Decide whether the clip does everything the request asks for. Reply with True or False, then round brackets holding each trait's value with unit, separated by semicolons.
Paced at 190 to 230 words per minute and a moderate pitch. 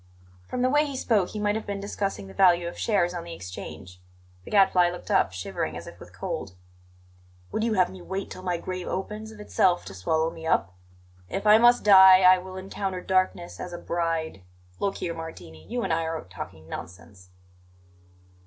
True (200 wpm; 180 Hz)